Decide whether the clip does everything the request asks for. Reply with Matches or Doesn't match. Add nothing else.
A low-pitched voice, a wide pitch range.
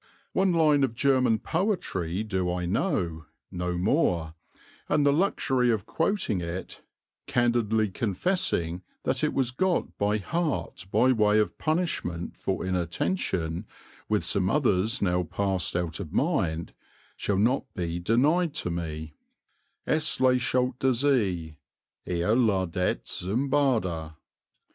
Matches